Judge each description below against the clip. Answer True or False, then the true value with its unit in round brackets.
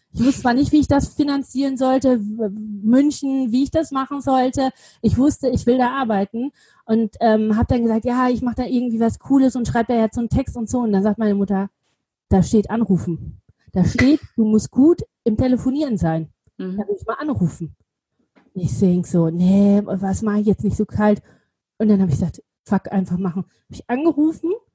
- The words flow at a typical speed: False (210 wpm)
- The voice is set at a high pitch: True (230 Hz)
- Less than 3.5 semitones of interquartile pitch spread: False (4.5 semitones)